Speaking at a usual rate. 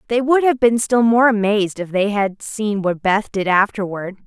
No: fast, 210 wpm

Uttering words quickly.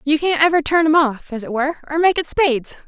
Yes: fast, 270 wpm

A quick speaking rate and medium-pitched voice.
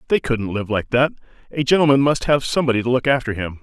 No: fast, 230 wpm; low, 130 Hz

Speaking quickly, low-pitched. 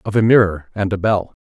Yes: fast, 250 wpm; low, 100 Hz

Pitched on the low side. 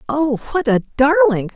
No: very high, 275 Hz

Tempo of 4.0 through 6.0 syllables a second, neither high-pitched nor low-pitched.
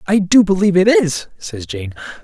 Yes: 5.1 syllables/s; medium, 175 Hz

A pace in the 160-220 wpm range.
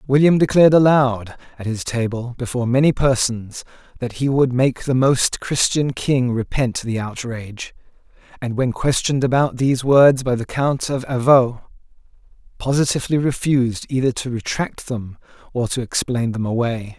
No: average, 150 wpm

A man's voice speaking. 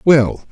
Yes: male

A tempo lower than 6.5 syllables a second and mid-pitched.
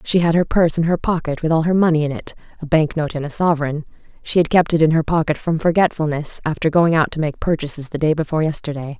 No: 6.6 syllables/s; medium, 160 Hz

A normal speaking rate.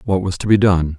No: fast, 305 wpm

